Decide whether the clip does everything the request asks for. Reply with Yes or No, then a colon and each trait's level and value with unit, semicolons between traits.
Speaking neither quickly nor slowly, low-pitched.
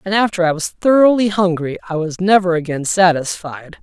No: average, 175 wpm; medium, 180 Hz